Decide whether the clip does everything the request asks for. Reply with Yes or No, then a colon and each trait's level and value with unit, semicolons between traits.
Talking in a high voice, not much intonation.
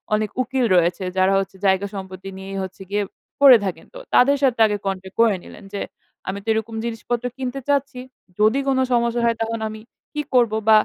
No: high, 220 Hz; average, 4.3 semitones